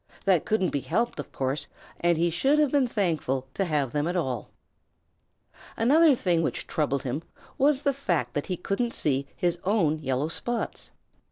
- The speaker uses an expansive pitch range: Yes, wide, 8.0 semitones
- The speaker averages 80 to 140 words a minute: No, average, 175 wpm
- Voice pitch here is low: No, medium, 175 Hz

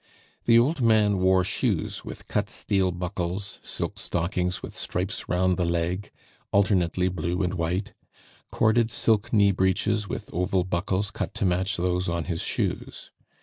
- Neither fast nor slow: Yes, average, 150 wpm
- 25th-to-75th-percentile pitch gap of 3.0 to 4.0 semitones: No, narrow, 2.4 semitones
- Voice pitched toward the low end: Yes, very low, 95 Hz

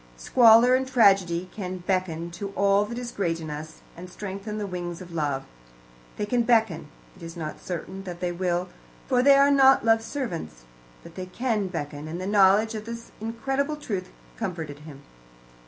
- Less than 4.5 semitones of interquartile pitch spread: No, average, 5.0 semitones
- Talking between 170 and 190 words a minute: Yes, average, 180 wpm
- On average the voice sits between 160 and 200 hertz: Yes, high, 190 Hz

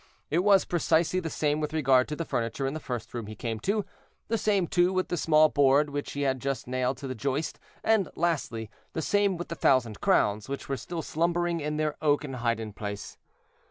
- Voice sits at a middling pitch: Yes, medium, 150 Hz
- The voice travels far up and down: No, average, 4.9 semitones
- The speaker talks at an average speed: No, fast, 210 wpm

